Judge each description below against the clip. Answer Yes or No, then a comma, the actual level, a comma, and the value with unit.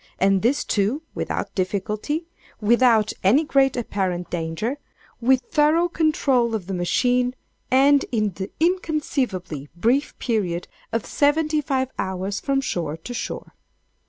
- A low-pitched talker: No, high, 240 Hz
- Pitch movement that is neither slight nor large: No, wide, 6.7 semitones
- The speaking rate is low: Yes, slow, 120 wpm